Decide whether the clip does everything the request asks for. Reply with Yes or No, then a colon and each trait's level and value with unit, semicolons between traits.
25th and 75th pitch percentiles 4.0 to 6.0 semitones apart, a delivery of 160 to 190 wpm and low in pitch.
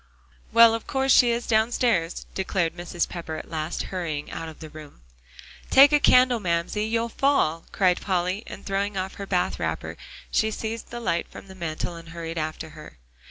No: wide, 5.4 semitones; average, 185 wpm; medium, 185 Hz